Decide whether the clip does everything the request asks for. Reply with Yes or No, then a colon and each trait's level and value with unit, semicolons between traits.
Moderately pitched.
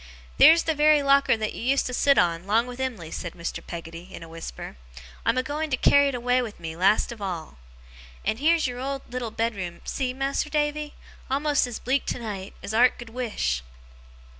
No: high, 245 Hz